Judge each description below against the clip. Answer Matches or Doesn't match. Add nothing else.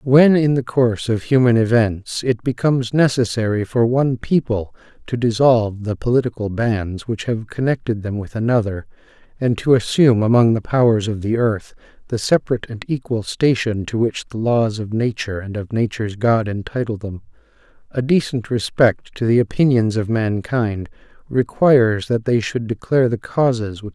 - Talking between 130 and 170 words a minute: Doesn't match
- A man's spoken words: Matches